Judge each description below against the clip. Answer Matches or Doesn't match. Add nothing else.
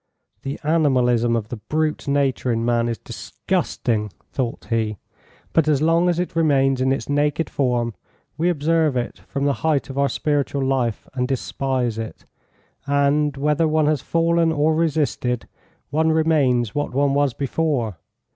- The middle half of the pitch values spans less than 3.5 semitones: Doesn't match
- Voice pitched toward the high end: Doesn't match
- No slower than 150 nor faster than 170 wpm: Matches